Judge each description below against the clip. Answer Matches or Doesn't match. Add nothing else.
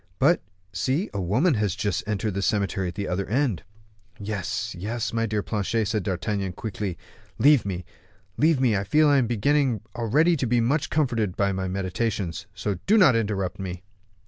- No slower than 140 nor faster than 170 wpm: Doesn't match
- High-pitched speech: Doesn't match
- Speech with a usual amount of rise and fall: Matches